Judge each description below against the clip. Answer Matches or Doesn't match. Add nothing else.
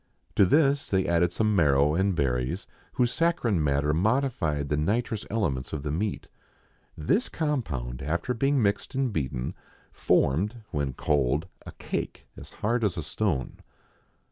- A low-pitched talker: Matches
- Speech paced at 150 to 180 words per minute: Doesn't match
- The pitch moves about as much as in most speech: Doesn't match